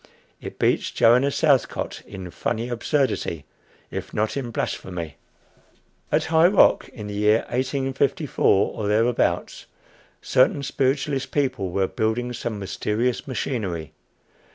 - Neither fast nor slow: No, slow, 115 wpm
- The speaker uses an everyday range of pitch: Yes, average, 4.5 semitones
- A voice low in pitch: Yes, low, 120 Hz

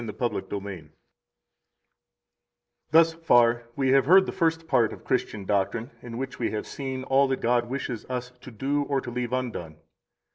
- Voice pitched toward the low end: Yes, low, 125 Hz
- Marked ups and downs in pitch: No, average, 3.0 semitones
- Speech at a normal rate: Yes, average, 180 wpm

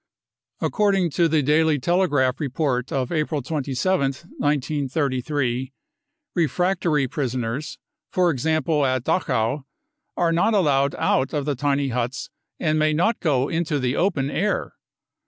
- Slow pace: Yes, slow, 125 wpm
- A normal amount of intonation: Yes, average, 3.7 semitones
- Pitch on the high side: No, medium, 145 Hz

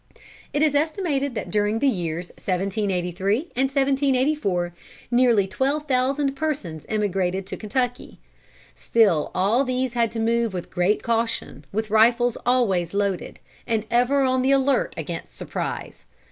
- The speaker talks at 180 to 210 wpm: No, slow, 135 wpm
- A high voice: Yes, high, 230 Hz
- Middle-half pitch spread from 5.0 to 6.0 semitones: Yes, wide, 5.5 semitones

